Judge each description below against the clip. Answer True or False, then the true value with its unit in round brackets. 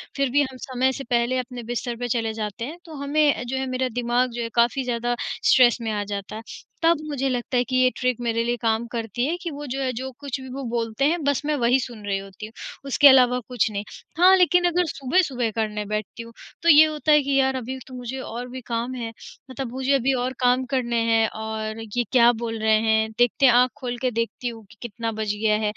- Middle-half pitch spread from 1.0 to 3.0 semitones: True (2.7 semitones)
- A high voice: True (245 Hz)